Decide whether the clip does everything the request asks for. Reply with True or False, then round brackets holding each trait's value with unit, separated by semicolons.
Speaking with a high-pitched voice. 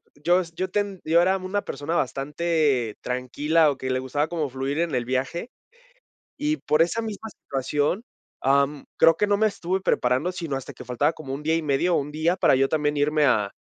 False (150 Hz)